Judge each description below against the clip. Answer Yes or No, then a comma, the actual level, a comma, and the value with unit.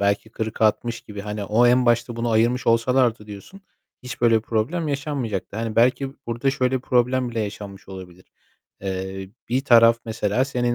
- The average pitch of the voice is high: No, low, 115 Hz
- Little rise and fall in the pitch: No, average, 3.0 semitones